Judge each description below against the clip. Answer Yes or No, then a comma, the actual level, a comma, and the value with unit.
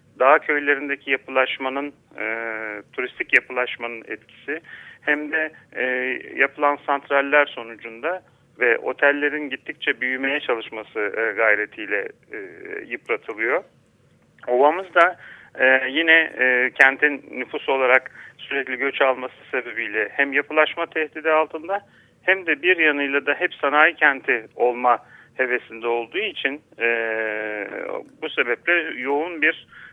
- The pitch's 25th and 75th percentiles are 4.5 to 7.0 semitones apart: No, average, 3.5 semitones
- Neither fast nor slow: Yes, average, 110 wpm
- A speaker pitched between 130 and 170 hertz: Yes, medium, 140 Hz